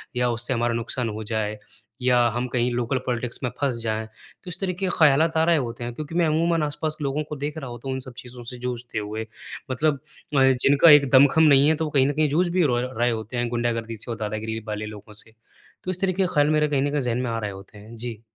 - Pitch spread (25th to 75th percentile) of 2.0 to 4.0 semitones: No, average, 4.5 semitones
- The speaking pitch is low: Yes, low, 125 Hz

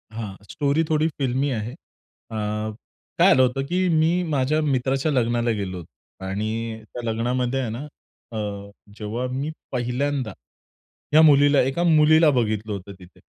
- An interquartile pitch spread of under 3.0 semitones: No, average, 4.5 semitones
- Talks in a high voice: No, low, 130 Hz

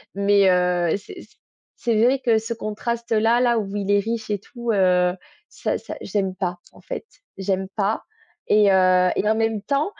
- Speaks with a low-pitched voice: No, high, 205 Hz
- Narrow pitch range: No, average, 3.2 semitones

